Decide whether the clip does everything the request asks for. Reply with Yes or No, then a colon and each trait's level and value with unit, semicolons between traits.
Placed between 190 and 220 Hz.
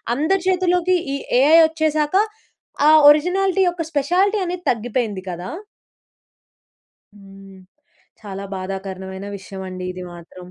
No: very high, 250 Hz